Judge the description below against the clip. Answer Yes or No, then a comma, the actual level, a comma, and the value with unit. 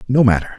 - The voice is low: Yes, low, 115 Hz